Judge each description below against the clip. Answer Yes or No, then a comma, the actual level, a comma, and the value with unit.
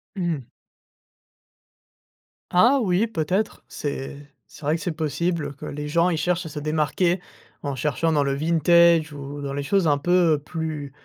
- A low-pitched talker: No, medium, 160 Hz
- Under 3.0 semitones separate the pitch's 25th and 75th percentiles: No, average, 3.3 semitones